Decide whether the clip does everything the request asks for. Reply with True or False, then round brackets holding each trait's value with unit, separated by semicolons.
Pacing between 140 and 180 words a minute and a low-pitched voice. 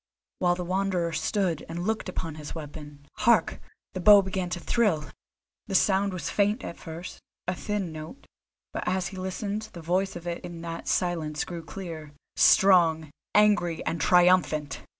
False (165 wpm; 175 Hz)